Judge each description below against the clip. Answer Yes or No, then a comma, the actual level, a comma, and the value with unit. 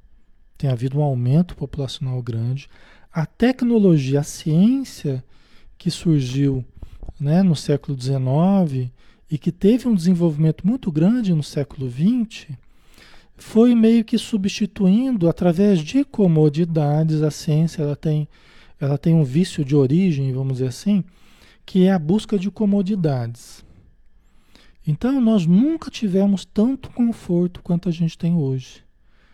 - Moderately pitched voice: Yes, medium, 165 Hz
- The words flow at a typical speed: Yes, average, 130 wpm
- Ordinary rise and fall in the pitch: No, wide, 6.1 semitones